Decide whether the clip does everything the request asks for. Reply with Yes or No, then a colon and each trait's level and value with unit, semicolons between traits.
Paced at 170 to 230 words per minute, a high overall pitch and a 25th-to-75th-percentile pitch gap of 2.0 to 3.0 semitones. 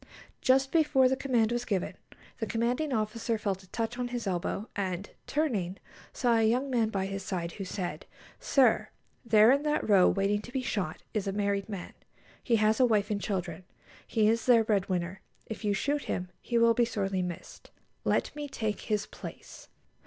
No: average, 190 wpm; high, 215 Hz; average, 3.7 semitones